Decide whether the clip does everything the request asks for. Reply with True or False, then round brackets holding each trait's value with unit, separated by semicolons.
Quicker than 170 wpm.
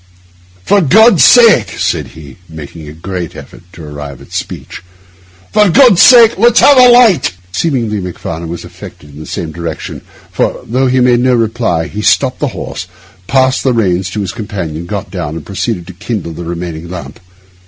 True (180 wpm)